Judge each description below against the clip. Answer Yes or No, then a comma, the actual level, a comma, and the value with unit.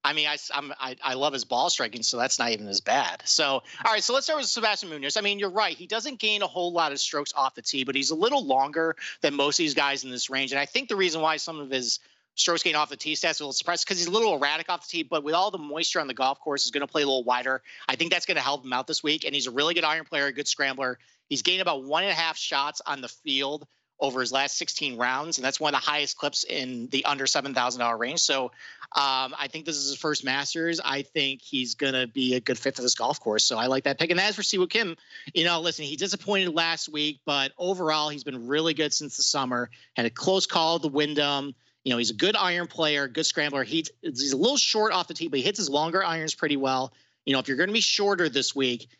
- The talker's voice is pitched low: No, medium, 150 Hz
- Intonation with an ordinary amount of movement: Yes, average, 3.7 semitones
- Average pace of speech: No, fast, 285 wpm